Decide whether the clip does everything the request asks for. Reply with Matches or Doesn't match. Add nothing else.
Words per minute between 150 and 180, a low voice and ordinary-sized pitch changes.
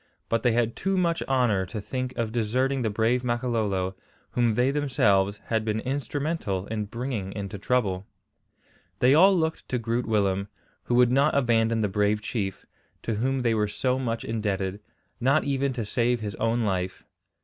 Matches